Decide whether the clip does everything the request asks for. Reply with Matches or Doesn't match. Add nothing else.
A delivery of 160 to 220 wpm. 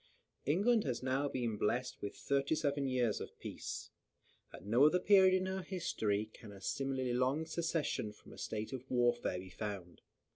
Matches